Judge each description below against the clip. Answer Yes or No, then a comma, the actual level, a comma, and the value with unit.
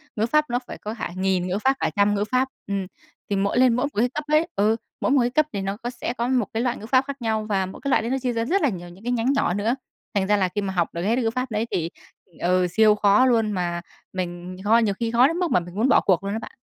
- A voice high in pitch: Yes, high, 220 Hz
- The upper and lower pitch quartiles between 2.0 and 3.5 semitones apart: No, average, 4.3 semitones